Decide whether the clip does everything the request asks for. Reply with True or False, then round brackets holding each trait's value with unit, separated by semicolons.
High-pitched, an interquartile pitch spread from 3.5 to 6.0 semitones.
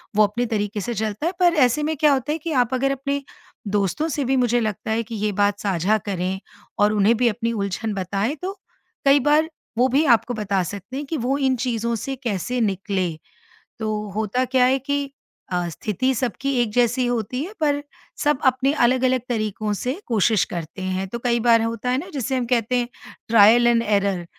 True (235 Hz; 4.0 semitones)